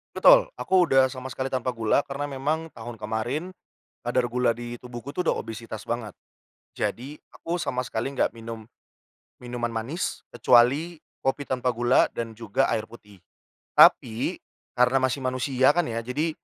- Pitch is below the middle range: Yes, low, 125 Hz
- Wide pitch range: No, average, 3.1 semitones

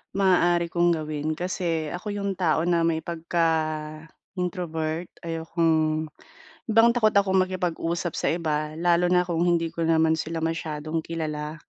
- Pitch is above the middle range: No, medium, 165 Hz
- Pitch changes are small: Yes, narrow, 1.9 semitones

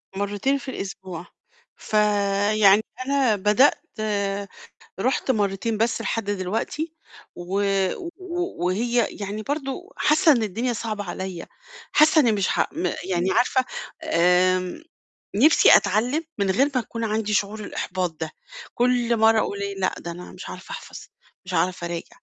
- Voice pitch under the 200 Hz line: No, high, 210 Hz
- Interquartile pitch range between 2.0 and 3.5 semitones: No, average, 4.3 semitones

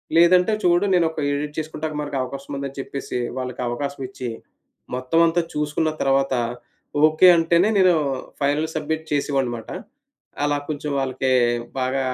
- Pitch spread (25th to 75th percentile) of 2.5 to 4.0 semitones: Yes, average, 3.0 semitones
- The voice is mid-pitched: Yes, medium, 145 Hz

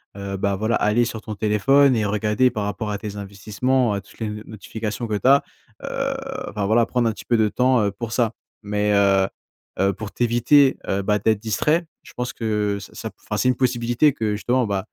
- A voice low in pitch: Yes, low, 110 Hz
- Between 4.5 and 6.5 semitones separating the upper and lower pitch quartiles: No, average, 3.1 semitones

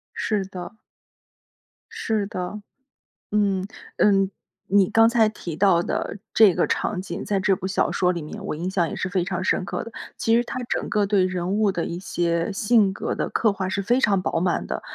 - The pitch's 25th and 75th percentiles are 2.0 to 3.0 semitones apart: Yes, narrow, 2.6 semitones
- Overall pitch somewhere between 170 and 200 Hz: Yes, high, 195 Hz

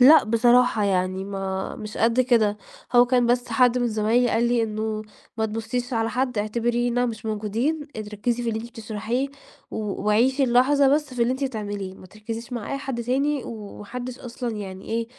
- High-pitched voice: Yes, high, 235 Hz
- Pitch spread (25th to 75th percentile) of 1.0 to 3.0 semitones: Yes, narrow, 2.6 semitones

